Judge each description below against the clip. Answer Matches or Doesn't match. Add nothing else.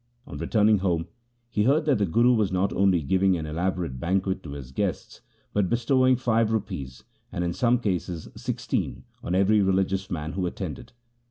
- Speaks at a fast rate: Doesn't match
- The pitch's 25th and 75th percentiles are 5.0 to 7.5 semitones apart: Doesn't match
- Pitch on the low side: Matches